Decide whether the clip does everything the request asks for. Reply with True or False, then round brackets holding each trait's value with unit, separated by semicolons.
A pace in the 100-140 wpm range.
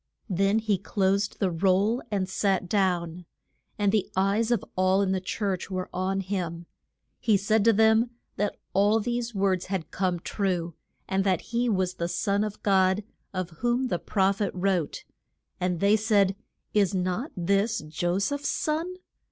False (165 wpm)